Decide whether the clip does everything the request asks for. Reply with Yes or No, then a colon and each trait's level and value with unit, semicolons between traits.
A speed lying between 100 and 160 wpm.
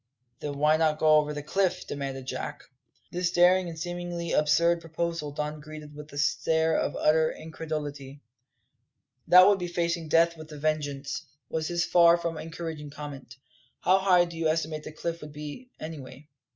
No: average, 170 wpm